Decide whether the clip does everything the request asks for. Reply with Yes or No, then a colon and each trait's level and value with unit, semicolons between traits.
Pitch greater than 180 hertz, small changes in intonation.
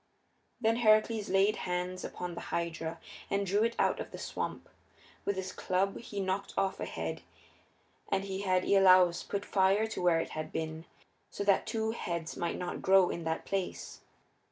Yes: high, 190 Hz; narrow, 2.2 semitones